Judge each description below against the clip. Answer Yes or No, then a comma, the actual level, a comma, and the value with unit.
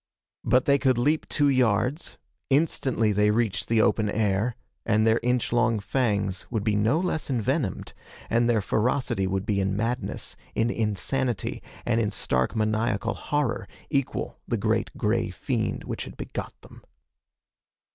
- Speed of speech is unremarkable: Yes, average, 150 wpm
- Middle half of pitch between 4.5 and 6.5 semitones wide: No, average, 3.5 semitones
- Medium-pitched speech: No, low, 115 Hz